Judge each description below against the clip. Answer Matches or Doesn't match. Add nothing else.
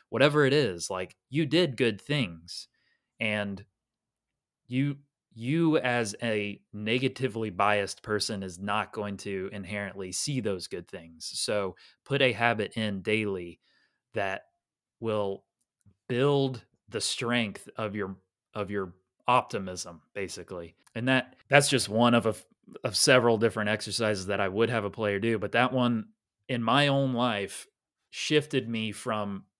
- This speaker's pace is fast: Doesn't match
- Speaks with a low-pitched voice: Matches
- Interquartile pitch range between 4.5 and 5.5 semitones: Doesn't match